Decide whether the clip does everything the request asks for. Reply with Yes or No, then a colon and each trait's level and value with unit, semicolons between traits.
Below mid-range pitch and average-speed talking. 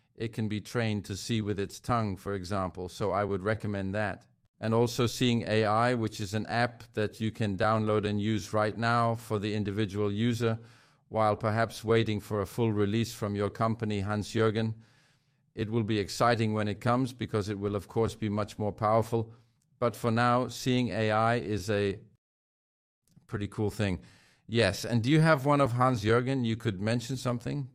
Yes: low, 110 Hz; average, 190 wpm